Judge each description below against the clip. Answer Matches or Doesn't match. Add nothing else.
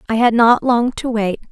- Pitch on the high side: Matches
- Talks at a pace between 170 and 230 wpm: Doesn't match